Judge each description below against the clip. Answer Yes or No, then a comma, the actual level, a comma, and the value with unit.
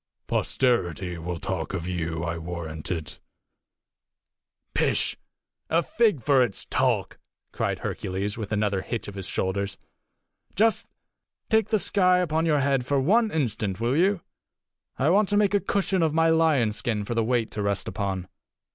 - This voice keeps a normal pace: Yes, average, 155 wpm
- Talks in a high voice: No, low, 115 Hz